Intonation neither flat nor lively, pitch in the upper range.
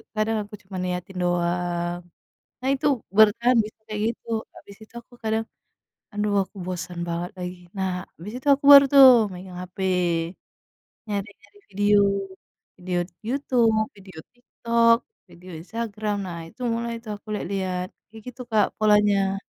Yes: average, 3.7 semitones; high, 205 Hz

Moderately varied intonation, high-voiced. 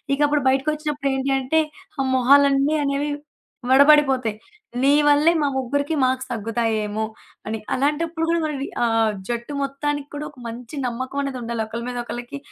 Yes: average, 3.3 semitones; very high, 275 Hz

